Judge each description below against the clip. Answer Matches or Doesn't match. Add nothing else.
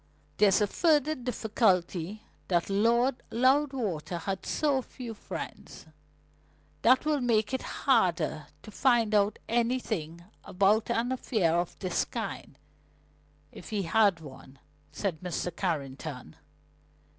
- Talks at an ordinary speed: Doesn't match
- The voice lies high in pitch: Matches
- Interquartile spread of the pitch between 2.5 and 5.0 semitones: Doesn't match